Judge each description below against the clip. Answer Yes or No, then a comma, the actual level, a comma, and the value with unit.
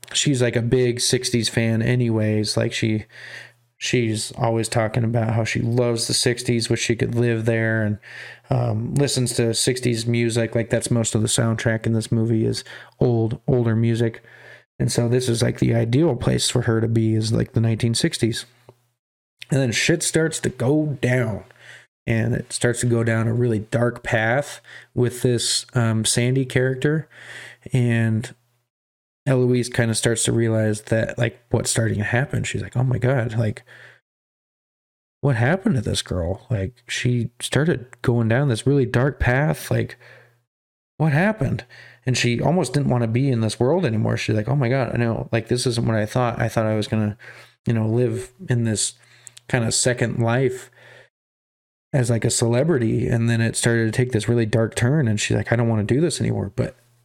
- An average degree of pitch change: No, narrow, 1.7 semitones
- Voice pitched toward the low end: Yes, low, 120 Hz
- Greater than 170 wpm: Yes, average, 190 wpm